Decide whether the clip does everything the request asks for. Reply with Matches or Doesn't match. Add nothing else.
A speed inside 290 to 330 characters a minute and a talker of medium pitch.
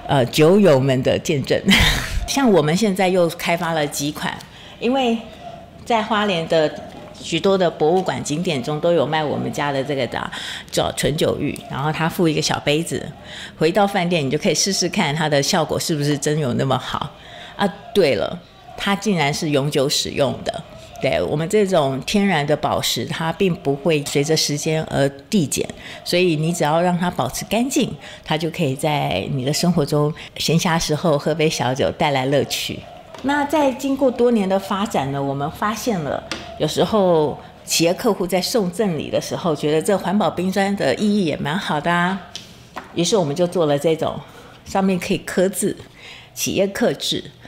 Doesn't match